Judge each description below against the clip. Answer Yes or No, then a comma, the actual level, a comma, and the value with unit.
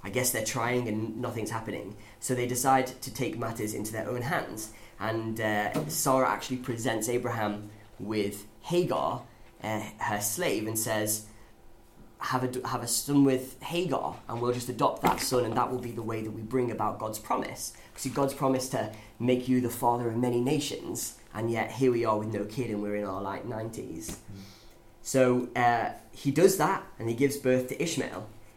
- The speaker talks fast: No, average, 190 wpm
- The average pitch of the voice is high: No, low, 115 Hz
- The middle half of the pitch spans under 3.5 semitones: Yes, average, 2.9 semitones